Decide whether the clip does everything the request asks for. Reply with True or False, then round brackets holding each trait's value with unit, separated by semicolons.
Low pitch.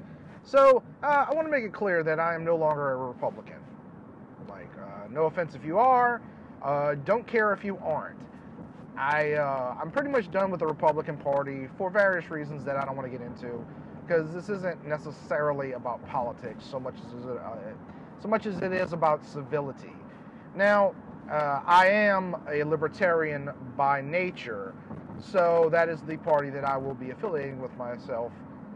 False (165 Hz)